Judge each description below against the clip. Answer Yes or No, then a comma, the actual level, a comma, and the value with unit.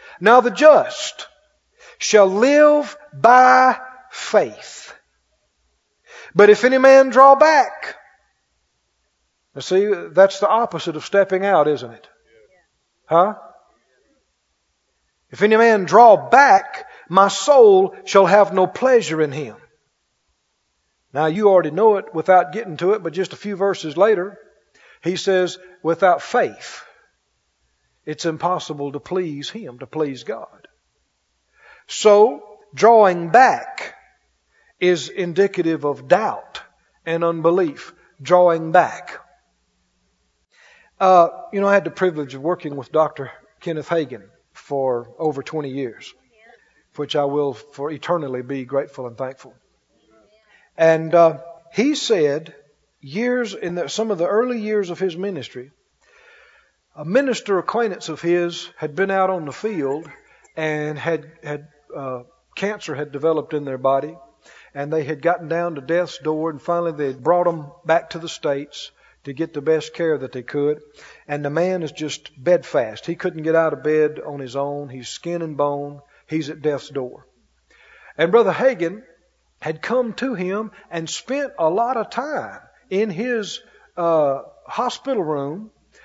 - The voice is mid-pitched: Yes, medium, 170 Hz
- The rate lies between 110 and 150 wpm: Yes, average, 140 wpm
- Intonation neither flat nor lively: No, wide, 5.9 semitones